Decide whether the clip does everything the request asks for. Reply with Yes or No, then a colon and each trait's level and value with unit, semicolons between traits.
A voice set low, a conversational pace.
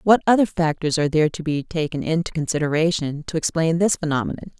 No: medium, 160 Hz; average, 185 wpm